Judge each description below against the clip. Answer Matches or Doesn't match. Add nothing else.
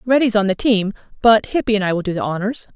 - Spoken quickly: Matches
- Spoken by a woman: Matches